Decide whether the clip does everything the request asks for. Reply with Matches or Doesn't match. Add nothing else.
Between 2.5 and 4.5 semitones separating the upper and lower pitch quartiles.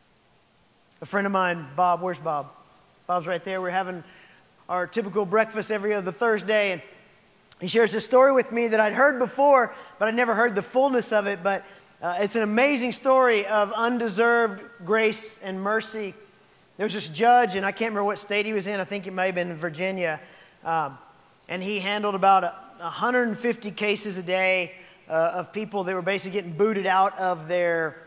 Matches